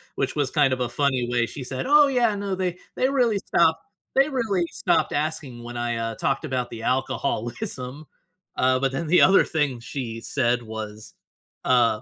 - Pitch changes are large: Yes, wide, 6.2 semitones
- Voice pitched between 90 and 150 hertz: Yes, low, 135 Hz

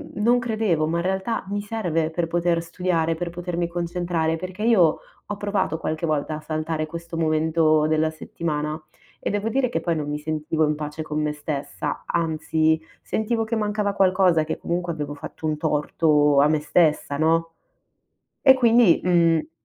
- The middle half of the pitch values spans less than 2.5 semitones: No, average, 2.9 semitones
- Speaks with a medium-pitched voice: Yes, medium, 165 Hz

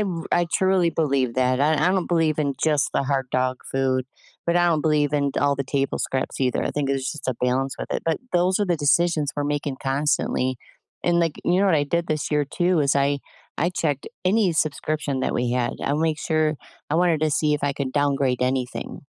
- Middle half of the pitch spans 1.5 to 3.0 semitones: No, average, 3.4 semitones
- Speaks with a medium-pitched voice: Yes, medium, 145 Hz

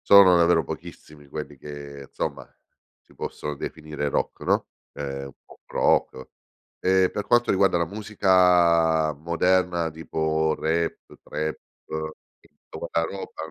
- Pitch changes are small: No, average, 3.2 semitones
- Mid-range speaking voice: No, very low, 80 Hz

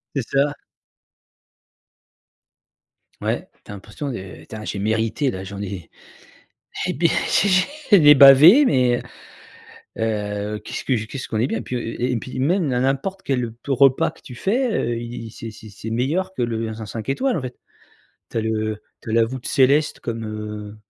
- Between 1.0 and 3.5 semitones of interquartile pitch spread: No, average, 4.3 semitones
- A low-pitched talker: Yes, low, 120 Hz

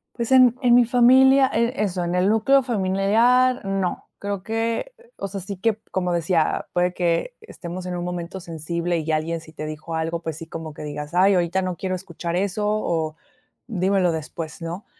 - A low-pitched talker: No, medium, 185 Hz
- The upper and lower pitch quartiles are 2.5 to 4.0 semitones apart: No, average, 4.7 semitones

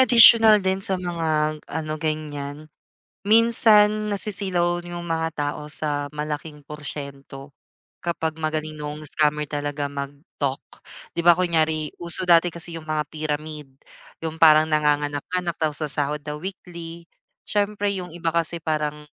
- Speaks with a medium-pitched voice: Yes, medium, 155 Hz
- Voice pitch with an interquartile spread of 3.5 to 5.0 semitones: No, narrow, 2.6 semitones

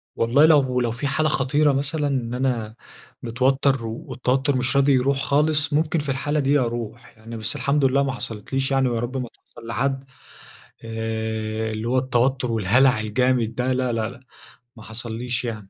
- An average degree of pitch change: Yes, average, 3.0 semitones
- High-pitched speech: No, low, 125 Hz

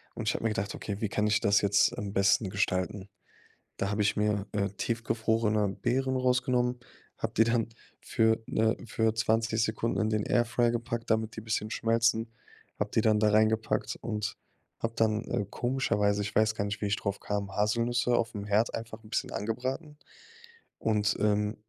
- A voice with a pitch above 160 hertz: No, low, 110 Hz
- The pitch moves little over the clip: Yes, narrow, 1.8 semitones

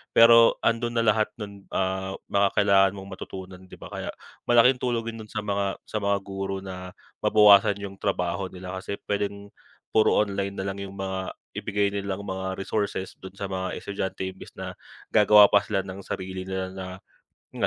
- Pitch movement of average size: No, narrow, 1.5 semitones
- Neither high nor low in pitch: No, low, 100 Hz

